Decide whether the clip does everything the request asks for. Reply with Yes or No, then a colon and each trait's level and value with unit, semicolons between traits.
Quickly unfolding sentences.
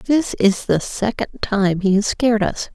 No: average, 195 wpm